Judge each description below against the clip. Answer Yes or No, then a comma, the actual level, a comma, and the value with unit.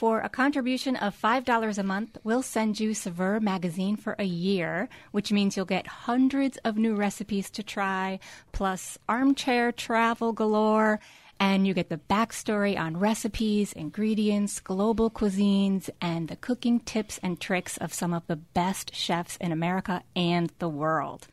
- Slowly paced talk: No, average, 160 wpm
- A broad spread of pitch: No, average, 3.3 semitones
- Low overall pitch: No, high, 205 Hz